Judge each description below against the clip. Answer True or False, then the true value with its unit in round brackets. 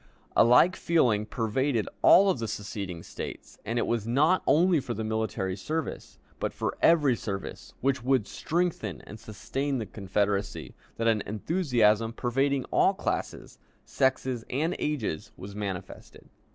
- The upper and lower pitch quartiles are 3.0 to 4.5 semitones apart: False (5.0 semitones)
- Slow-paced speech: False (145 wpm)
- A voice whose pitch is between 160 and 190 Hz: False (115 Hz)